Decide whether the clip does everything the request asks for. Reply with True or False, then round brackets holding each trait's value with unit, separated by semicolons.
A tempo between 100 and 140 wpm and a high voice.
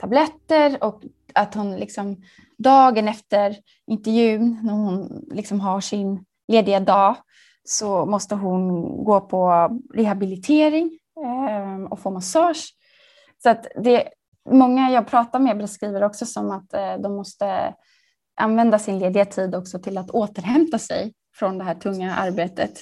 True (135 wpm; 210 Hz)